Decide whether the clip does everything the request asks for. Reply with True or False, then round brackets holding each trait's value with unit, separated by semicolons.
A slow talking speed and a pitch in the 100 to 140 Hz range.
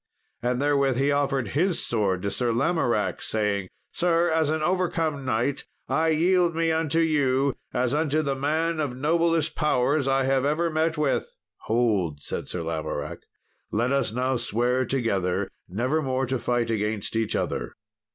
False (155 wpm; 135 Hz)